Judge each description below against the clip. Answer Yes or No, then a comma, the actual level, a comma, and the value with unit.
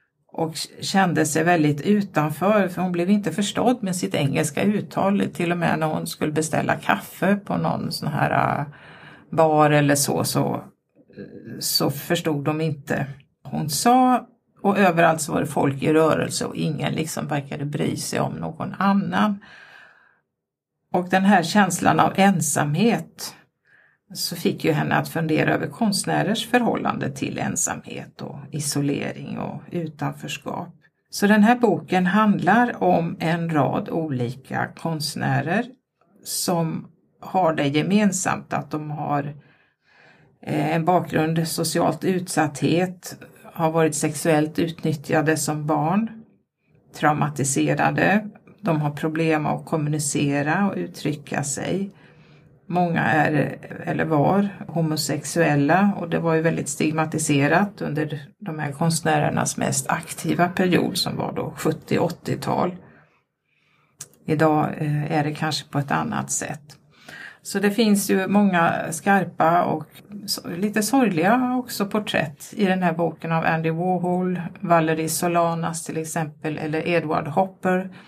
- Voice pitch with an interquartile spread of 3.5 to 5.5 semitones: Yes, average, 3.9 semitones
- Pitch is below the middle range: No, medium, 165 Hz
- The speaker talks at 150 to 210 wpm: No, average, 130 wpm